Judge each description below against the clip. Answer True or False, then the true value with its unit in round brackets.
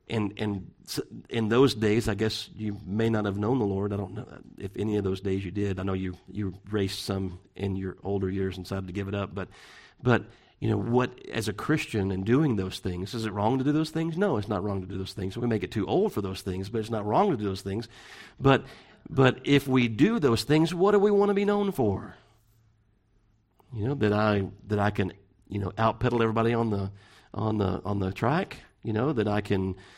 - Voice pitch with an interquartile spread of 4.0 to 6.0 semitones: False (2.9 semitones)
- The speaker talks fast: True (245 wpm)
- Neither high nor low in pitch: False (105 Hz)